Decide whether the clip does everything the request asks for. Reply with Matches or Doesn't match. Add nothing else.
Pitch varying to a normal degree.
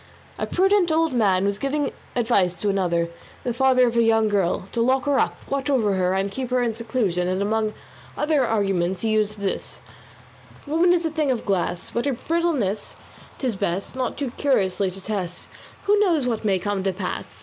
Doesn't match